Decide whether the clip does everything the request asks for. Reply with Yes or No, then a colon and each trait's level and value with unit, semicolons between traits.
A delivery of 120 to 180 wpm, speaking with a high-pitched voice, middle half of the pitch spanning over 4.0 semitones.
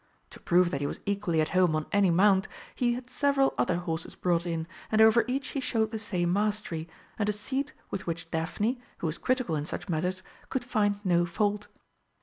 No: fast, 205 wpm; high, 195 Hz; average, 4.5 semitones